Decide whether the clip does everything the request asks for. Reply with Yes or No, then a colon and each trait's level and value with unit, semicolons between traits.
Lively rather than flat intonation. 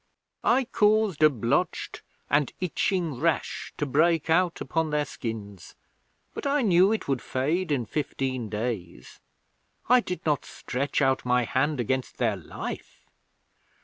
Yes: wide, 6.1 semitones